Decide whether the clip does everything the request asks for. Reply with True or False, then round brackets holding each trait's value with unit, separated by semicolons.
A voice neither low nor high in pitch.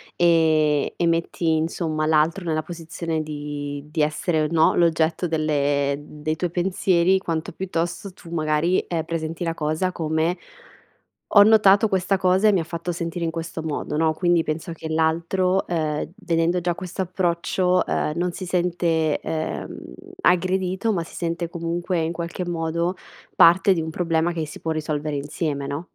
True (165 Hz)